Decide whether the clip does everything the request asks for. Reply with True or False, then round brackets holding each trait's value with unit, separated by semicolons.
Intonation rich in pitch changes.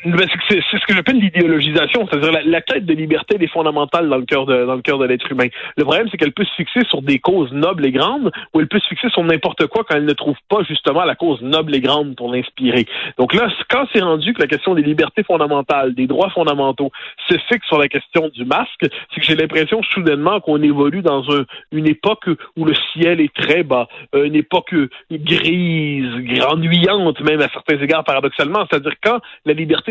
False (3.8 semitones)